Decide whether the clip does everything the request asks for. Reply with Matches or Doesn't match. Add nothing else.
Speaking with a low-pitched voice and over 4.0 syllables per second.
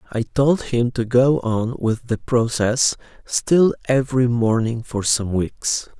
Doesn't match